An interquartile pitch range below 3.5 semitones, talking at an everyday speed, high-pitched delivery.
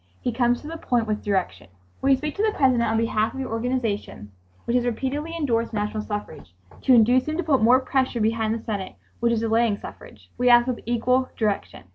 No: average, 3.0 semitones; fast, 215 wpm; high, 235 Hz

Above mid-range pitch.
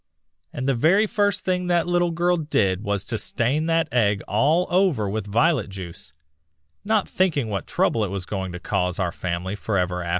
No: low, 115 Hz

